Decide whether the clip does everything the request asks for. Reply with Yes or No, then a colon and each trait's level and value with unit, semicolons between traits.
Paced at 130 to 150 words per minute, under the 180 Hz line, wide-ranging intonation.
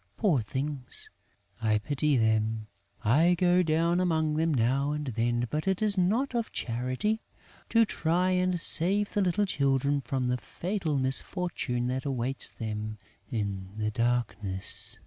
Yes: average, 145 wpm; medium, 140 Hz; wide, 6.9 semitones